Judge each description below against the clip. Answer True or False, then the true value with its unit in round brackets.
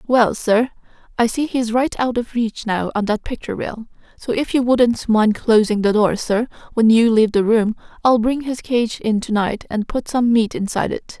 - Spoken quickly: True (220 wpm)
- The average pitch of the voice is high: True (230 Hz)